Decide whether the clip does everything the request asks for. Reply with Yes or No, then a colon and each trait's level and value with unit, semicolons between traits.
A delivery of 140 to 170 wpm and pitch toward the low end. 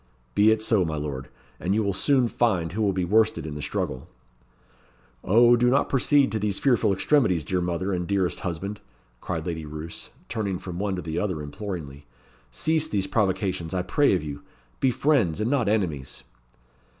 No: average, 185 wpm; very low, 95 Hz